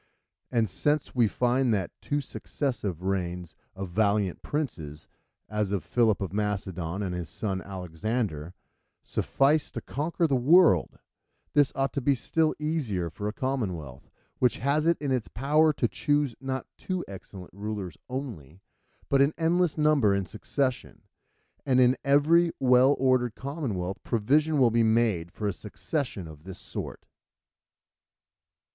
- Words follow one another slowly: No, average, 145 wpm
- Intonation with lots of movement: Yes, wide, 6.6 semitones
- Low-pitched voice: Yes, low, 120 Hz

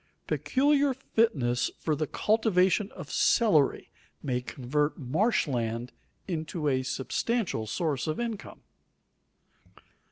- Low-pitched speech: No, medium, 155 Hz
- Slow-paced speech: Yes, slow, 100 wpm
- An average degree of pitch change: No, wide, 9.0 semitones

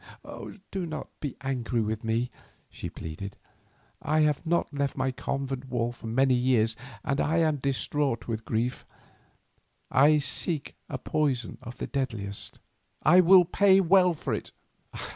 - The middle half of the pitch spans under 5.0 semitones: Yes, average, 4.6 semitones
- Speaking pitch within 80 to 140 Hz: Yes, low, 135 Hz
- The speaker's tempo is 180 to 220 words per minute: No, average, 145 wpm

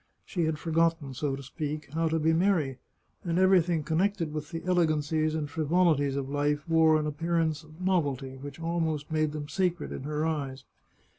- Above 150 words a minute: Yes, average, 175 wpm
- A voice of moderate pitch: Yes, medium, 155 Hz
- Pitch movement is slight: Yes, narrow, 2.2 semitones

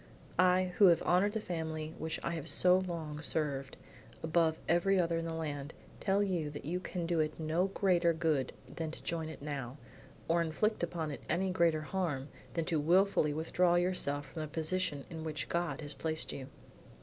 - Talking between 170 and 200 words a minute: Yes, average, 190 wpm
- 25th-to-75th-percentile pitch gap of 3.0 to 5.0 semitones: No, narrow, 2.6 semitones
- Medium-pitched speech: Yes, medium, 165 Hz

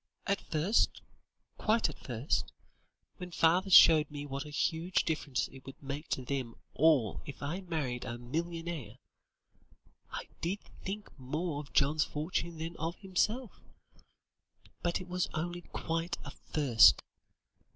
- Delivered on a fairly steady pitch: No, average, 4.0 semitones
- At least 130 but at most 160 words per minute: Yes, average, 140 wpm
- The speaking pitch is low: No, medium, 160 Hz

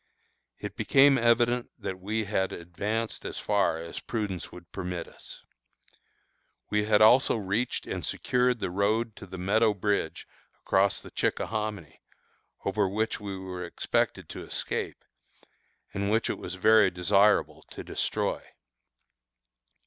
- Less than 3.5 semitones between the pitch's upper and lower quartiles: Yes, average, 2.9 semitones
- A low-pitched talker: Yes, low, 105 Hz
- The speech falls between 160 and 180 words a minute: No, slow, 135 wpm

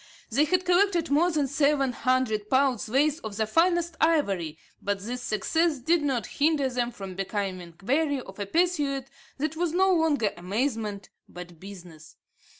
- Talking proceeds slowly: No, average, 155 wpm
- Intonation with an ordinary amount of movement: No, wide, 7.7 semitones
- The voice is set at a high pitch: Yes, very high, 265 Hz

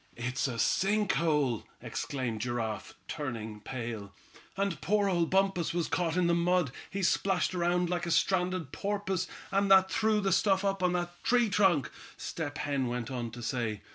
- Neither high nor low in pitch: Yes, medium, 170 Hz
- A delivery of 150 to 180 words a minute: Yes, average, 170 wpm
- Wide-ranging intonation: Yes, wide, 7.4 semitones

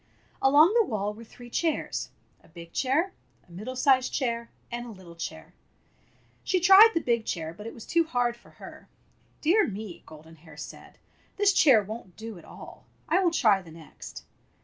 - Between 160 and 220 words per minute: Yes, average, 190 wpm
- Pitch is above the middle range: Yes, high, 235 Hz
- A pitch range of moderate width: No, wide, 8.3 semitones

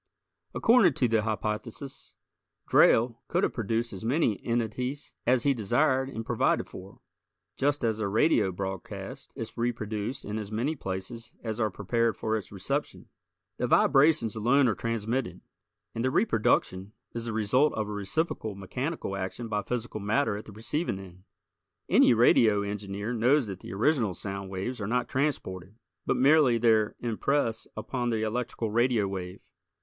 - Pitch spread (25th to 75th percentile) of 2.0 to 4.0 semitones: Yes, average, 3.6 semitones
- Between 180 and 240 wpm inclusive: No, average, 155 wpm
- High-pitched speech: No, low, 115 Hz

